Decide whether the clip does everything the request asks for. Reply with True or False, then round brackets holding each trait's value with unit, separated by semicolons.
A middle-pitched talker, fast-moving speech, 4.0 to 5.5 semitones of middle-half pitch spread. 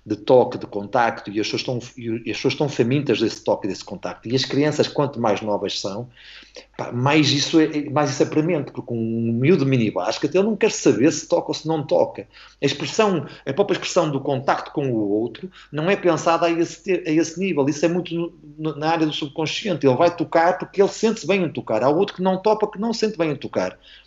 True (155 Hz; 235 wpm; 4.9 semitones)